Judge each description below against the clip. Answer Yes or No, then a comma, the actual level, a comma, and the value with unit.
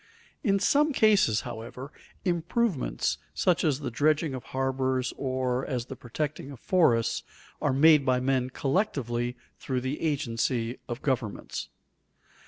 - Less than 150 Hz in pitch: Yes, low, 135 Hz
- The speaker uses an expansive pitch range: No, average, 3.7 semitones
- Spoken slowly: Yes, slow, 130 wpm